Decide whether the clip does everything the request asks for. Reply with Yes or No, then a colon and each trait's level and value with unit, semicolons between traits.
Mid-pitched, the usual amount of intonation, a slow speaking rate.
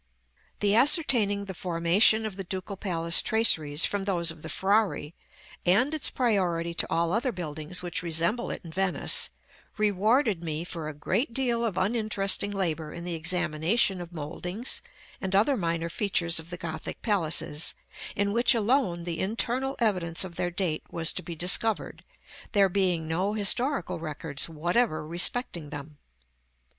No: medium, 180 Hz; average, 4.3 semitones; average, 155 wpm